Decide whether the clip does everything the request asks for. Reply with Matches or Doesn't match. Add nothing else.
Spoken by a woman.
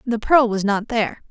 Matches